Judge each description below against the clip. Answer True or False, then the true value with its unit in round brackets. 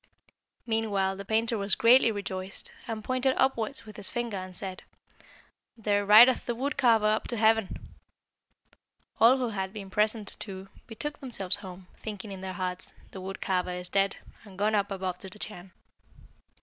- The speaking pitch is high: True (210 Hz)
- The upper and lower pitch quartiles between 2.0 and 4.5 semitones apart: True (3.0 semitones)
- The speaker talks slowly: False (170 wpm)